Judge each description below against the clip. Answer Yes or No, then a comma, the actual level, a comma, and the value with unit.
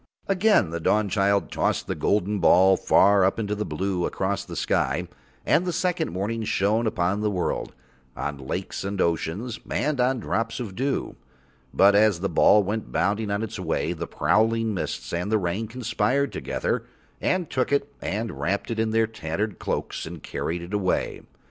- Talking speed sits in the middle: Yes, average, 175 wpm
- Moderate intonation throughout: Yes, average, 3.5 semitones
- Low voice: Yes, low, 105 Hz